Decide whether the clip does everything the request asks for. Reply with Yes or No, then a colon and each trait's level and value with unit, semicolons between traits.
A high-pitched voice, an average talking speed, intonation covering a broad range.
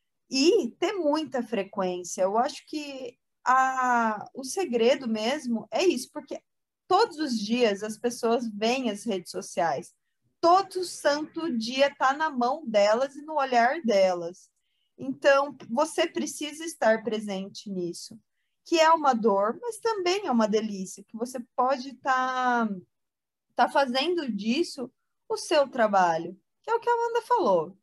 Yes: very high, 255 Hz; average, 140 wpm; wide, 5.9 semitones